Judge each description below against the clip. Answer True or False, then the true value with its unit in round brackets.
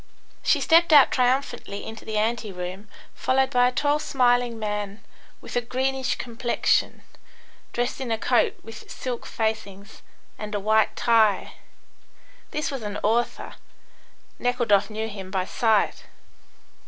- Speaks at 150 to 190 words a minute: False (135 wpm)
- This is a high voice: True (230 Hz)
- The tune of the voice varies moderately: True (3.1 semitones)